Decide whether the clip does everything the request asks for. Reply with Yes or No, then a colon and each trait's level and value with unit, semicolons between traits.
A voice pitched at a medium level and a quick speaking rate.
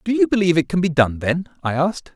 Yes: medium, 160 Hz; fast, 280 wpm